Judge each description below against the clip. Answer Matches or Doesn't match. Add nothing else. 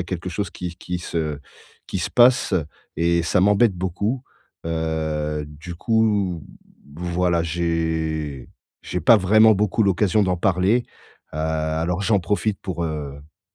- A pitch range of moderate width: Matches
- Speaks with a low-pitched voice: Matches